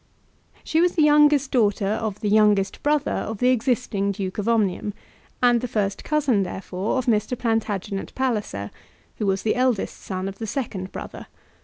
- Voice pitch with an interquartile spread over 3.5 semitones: Yes, average, 4.2 semitones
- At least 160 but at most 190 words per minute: Yes, average, 170 wpm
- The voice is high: Yes, high, 220 Hz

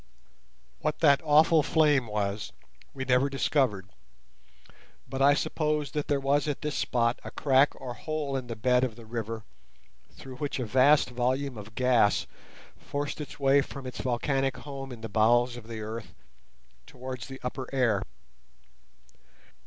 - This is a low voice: Yes, low, 130 Hz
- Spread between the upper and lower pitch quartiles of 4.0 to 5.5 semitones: No, average, 3.1 semitones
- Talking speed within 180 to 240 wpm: No, average, 155 wpm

